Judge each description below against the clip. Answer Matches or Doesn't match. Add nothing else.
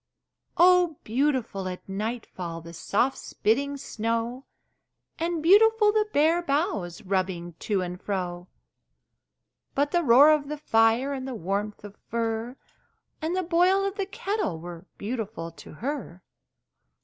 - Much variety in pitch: Matches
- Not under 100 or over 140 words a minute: Matches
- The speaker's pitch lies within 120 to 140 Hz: Doesn't match